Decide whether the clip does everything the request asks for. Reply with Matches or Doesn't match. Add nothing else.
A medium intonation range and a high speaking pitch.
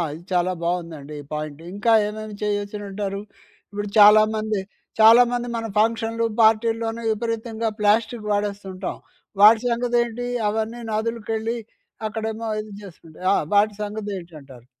Doesn't match